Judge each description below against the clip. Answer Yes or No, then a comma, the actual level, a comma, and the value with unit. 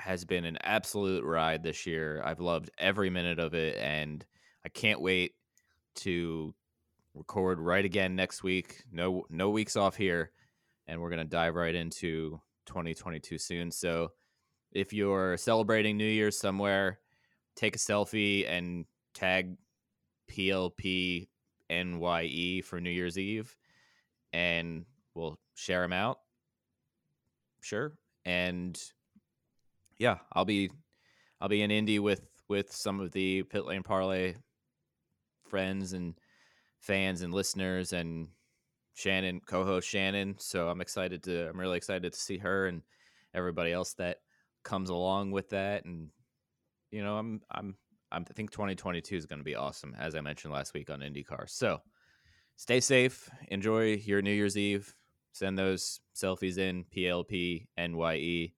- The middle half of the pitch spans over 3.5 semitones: No, average, 2.8 semitones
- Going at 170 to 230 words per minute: No, average, 145 wpm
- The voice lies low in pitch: Yes, very low, 95 Hz